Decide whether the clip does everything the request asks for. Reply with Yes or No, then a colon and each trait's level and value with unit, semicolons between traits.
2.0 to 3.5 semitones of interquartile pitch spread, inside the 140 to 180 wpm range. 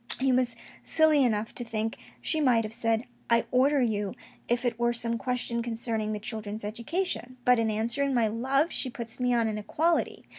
No: narrow, 2.4 semitones; average, 195 wpm